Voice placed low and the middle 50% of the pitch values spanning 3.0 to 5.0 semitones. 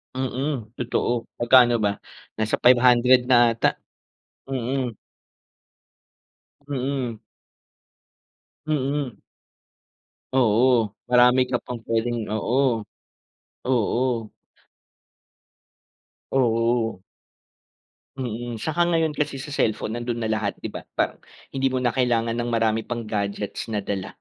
No: low, 120 Hz; narrow, 2.5 semitones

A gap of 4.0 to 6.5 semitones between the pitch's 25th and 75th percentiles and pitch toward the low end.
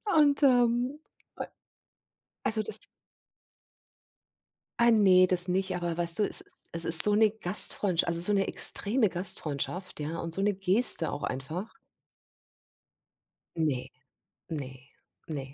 No: average, 4.3 semitones; medium, 185 Hz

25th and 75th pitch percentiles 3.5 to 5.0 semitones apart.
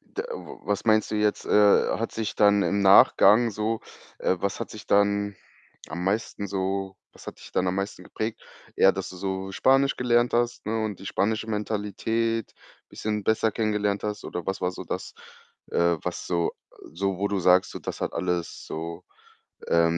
No: narrow, 2.5 semitones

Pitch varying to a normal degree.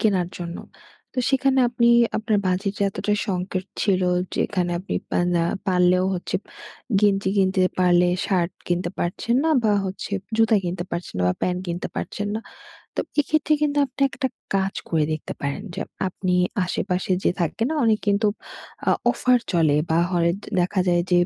Yes: average, 3.3 semitones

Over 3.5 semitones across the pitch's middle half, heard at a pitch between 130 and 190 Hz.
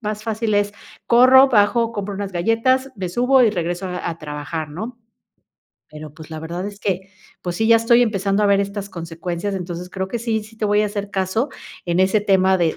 No: average, 4.0 semitones; high, 200 Hz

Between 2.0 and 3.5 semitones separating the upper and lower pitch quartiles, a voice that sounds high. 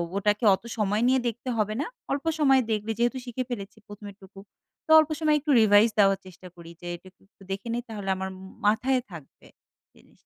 No: average, 4.0 semitones; high, 210 Hz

